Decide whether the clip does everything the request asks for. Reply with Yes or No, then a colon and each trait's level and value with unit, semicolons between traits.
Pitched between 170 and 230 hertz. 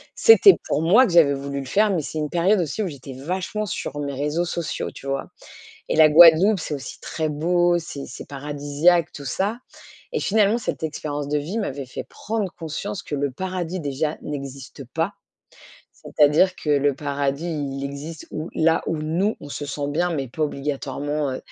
No: medium, 155 Hz